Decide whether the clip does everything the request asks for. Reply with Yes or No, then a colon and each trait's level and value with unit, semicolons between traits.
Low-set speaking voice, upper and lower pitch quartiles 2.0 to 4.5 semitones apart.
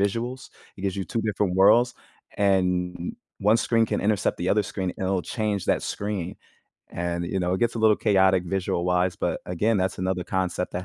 Yes: very low, 95 Hz; average, 2.7 semitones